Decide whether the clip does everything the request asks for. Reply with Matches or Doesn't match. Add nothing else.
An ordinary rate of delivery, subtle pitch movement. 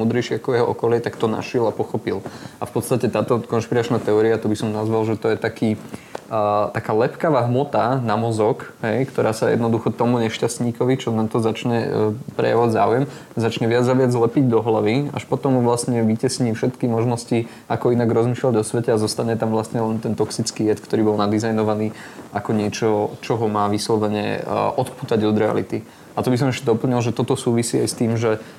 Doesn't match